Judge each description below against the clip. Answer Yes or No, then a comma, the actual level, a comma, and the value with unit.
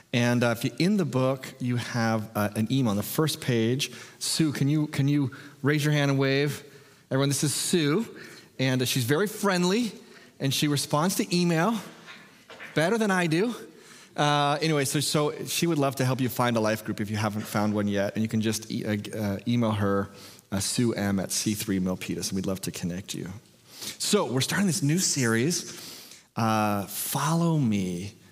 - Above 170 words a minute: Yes, average, 200 wpm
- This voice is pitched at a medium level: No, low, 130 Hz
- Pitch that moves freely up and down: Yes, wide, 5.8 semitones